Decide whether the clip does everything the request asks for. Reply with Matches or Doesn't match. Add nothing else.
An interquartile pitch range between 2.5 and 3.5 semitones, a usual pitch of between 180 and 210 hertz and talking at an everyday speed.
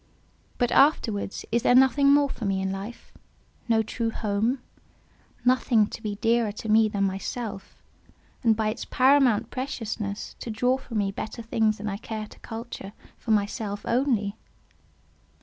Doesn't match